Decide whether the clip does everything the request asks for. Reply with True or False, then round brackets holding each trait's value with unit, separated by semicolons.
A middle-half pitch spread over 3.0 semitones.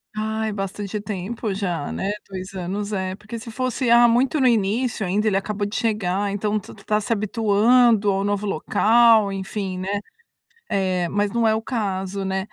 False (2.4 semitones)